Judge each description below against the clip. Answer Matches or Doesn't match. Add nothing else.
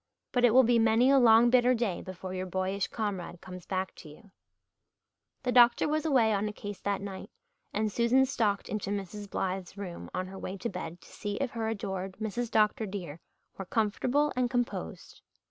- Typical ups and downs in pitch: Matches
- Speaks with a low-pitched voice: Doesn't match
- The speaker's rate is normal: Matches